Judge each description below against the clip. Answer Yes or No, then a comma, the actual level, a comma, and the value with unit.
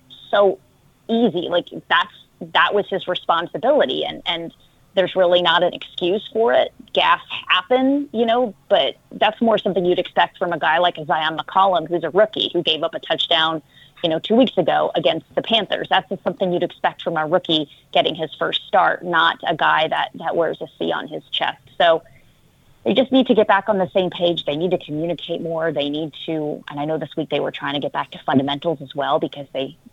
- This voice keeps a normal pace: No, fast, 215 wpm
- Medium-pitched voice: Yes, medium, 175 Hz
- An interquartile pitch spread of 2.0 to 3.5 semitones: No, average, 4.0 semitones